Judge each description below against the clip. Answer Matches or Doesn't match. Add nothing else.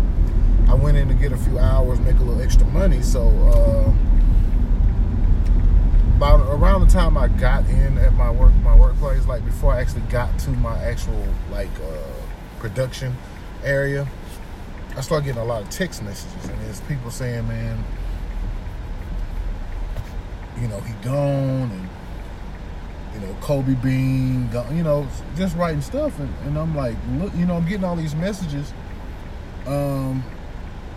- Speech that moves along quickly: Doesn't match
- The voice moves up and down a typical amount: Doesn't match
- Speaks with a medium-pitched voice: Doesn't match